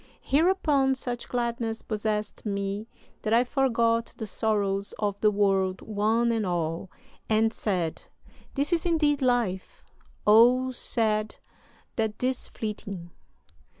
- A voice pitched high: Yes, high, 220 Hz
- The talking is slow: Yes, slow, 115 wpm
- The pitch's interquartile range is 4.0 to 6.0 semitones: No, average, 3.4 semitones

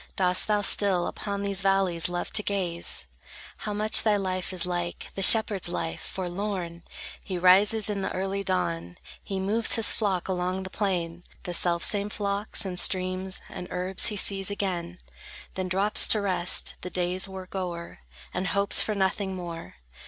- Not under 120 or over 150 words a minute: No, average, 165 wpm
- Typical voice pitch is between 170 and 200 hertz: Yes, high, 190 Hz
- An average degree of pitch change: No, narrow, 2.1 semitones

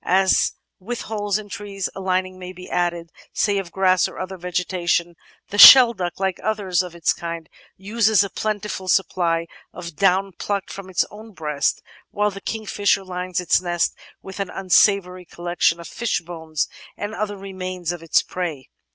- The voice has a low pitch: No, medium, 185 Hz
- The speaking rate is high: No, average, 170 wpm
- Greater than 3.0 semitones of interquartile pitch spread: No, narrow, 2.4 semitones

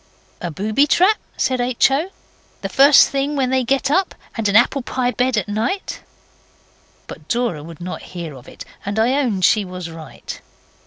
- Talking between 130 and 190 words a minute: Yes, average, 180 wpm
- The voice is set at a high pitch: Yes, high, 240 Hz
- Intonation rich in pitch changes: Yes, wide, 6.5 semitones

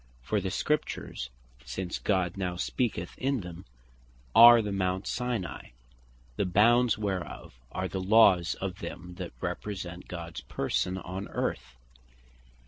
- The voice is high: No, very low, 95 Hz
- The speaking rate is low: Yes, slow, 130 wpm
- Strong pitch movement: No, average, 3.1 semitones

